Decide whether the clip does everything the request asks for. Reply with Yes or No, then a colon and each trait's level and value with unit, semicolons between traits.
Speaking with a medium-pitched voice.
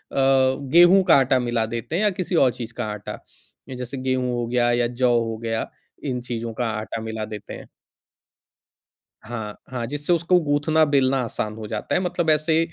No: low, 125 Hz